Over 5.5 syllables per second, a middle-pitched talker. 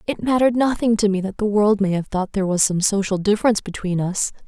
No: 6.4 syllables/s; high, 205 Hz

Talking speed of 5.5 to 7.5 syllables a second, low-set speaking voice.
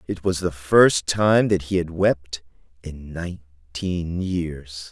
No: 3.4 syllables/s; very low, 85 Hz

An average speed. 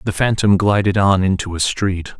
Yes: average, 190 wpm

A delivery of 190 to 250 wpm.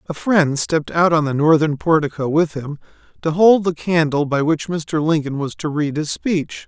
Yes: fast, 205 wpm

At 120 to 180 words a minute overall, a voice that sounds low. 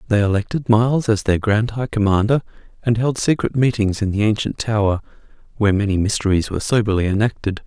Yes: average, 170 wpm; low, 110 Hz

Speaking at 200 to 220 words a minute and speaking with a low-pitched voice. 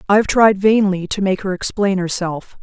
No: fast, 205 wpm; high, 195 Hz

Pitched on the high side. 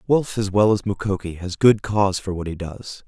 No: low, 100 Hz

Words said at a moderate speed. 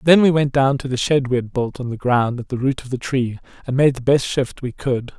No: fast, 300 wpm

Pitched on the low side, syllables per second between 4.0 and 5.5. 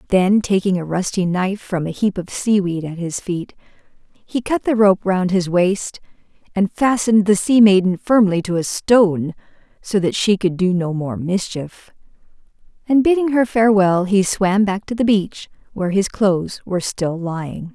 No: high, 195 Hz; 4.8 syllables/s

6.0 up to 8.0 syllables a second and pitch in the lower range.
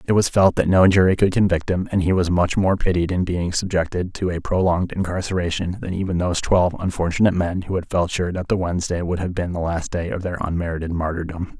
Yes: 6.2 syllables/s; very low, 90 Hz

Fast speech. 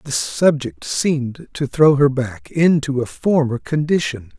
No: average, 150 wpm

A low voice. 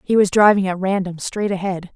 No: high, 190 Hz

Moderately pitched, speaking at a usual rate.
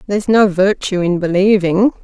No: high, 195 Hz; average, 150 wpm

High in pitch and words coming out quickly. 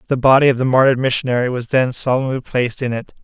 No: low, 125 Hz; fast, 225 wpm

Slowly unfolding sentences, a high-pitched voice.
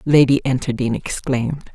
No: slow, 105 wpm; low, 130 Hz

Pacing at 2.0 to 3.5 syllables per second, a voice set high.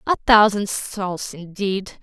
Yes: 3.4 syllables/s; high, 200 Hz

